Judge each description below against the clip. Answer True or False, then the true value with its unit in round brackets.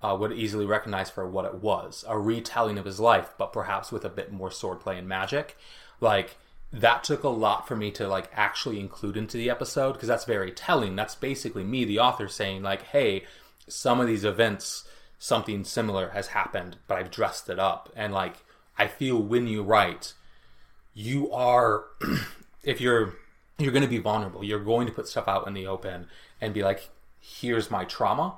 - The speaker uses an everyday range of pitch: True (3.2 semitones)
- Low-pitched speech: True (105 Hz)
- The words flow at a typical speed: True (190 wpm)